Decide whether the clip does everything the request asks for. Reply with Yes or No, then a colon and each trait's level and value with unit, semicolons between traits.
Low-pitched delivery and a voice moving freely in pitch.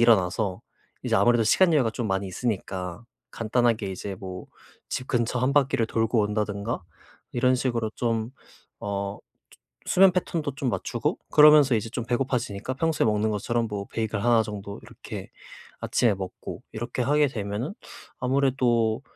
No: low, 115 Hz; average, 3.7 semitones